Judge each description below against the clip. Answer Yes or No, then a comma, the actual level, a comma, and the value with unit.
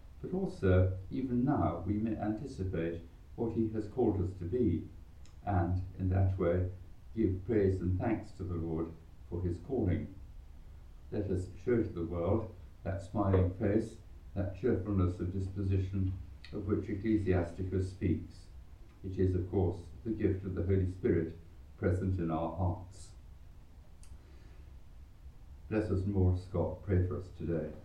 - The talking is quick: No, average, 145 wpm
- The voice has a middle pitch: No, very low, 95 Hz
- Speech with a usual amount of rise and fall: Yes, average, 3.3 semitones